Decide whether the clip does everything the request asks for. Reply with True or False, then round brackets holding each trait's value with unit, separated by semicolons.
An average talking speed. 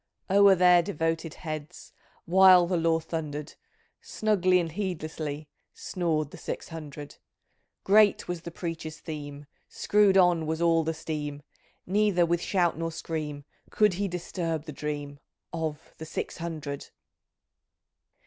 False (130 wpm)